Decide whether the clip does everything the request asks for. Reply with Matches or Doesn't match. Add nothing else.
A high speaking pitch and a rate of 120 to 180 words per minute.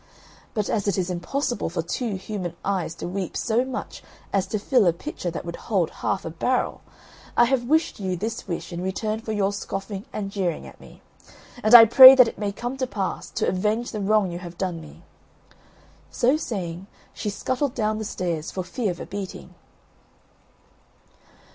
Doesn't match